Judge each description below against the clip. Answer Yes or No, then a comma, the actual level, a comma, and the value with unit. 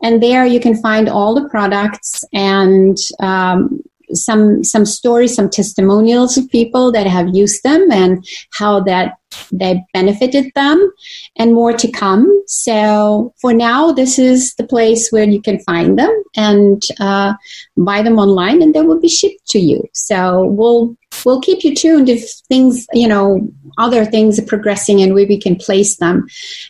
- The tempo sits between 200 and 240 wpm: No, average, 170 wpm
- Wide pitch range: No, average, 4.2 semitones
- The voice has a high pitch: Yes, high, 220 Hz